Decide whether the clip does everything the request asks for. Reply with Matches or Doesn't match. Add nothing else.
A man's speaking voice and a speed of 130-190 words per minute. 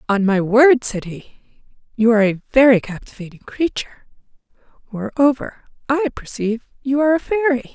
Doesn't match